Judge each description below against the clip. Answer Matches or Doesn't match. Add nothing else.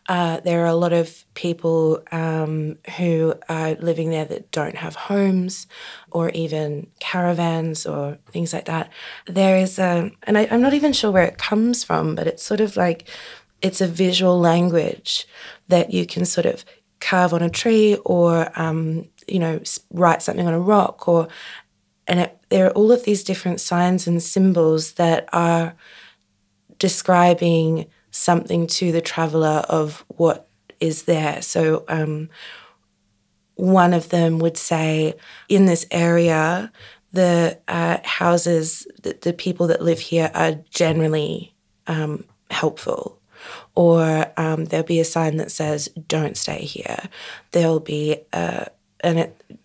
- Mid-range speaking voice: Matches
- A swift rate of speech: Doesn't match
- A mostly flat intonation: Matches